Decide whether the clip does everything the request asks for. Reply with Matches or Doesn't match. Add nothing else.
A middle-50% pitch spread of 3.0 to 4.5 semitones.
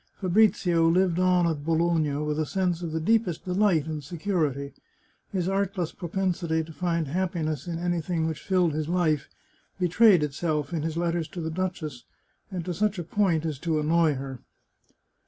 Doesn't match